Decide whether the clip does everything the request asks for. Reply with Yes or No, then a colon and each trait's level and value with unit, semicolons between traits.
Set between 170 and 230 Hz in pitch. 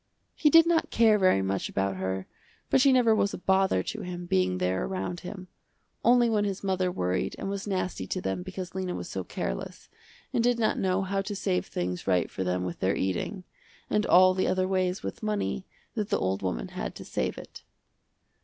Yes: medium, 185 Hz